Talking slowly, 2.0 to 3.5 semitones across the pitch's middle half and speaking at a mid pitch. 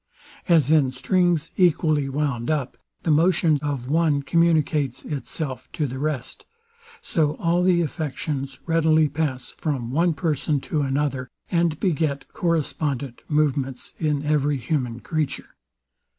Yes: slow, 125 wpm; average, 2.9 semitones; medium, 150 Hz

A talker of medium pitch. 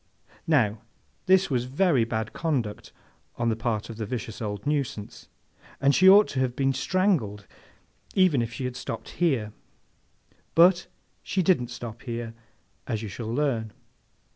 No: low, 125 Hz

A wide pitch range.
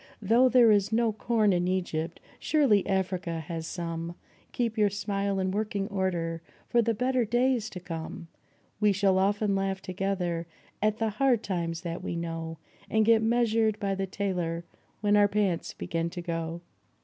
No: average, 4.1 semitones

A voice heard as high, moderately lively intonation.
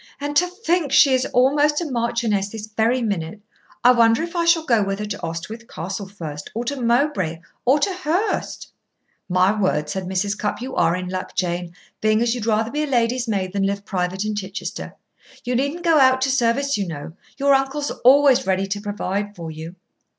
No: high, 225 Hz; wide, 5.8 semitones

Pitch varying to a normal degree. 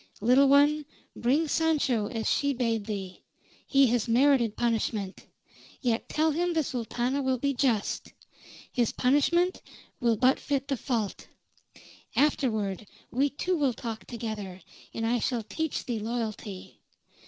Yes: average, 4.1 semitones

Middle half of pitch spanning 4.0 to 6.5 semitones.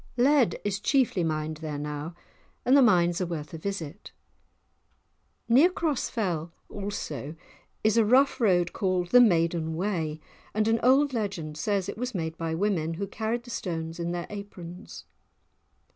Yes: wide, 5.5 semitones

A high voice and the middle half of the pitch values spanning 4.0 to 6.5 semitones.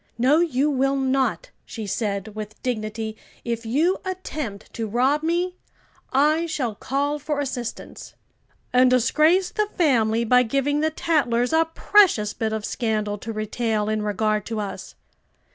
Yes: very high, 250 Hz; wide, 5.6 semitones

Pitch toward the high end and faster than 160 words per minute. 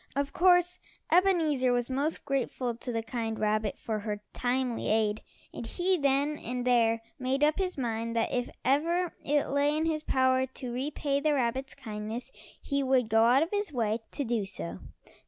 Yes: very high, 260 Hz; average, 180 wpm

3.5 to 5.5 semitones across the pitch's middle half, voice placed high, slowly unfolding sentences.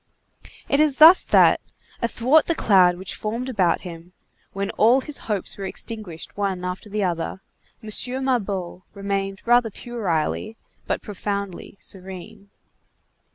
Yes: average, 4.0 semitones; high, 200 Hz; slow, 130 wpm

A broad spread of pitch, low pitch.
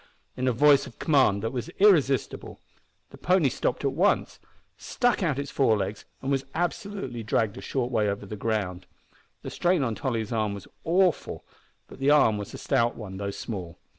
Yes: wide, 5.7 semitones; low, 125 Hz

